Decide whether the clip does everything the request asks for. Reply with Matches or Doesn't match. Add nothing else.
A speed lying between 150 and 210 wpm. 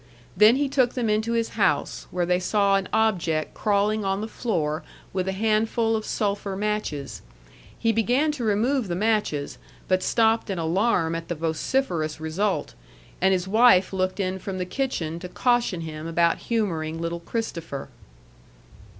Matches